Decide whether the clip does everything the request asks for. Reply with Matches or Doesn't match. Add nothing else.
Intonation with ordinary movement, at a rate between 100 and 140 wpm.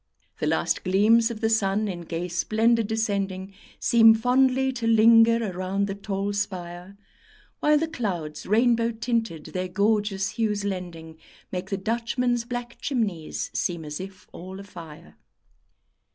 Matches